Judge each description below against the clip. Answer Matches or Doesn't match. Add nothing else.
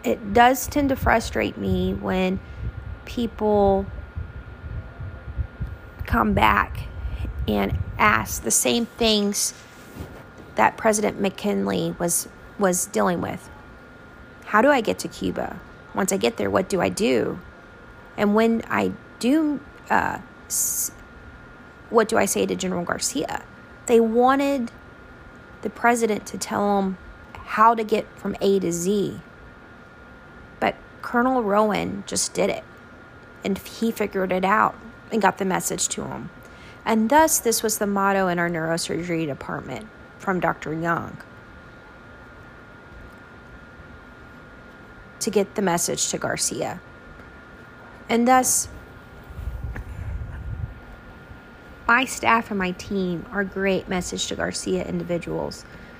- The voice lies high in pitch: Matches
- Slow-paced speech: Matches